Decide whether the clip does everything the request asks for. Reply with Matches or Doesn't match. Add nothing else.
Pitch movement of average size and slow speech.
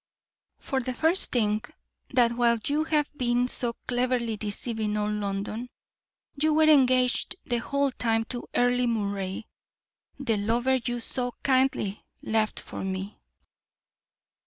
Matches